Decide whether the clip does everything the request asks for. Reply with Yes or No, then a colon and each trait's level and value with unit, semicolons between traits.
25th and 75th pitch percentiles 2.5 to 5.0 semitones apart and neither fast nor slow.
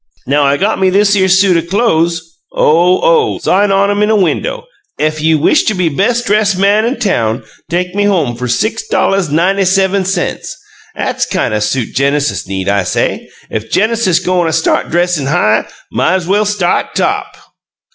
Yes: average, 4.7 semitones; average, 175 wpm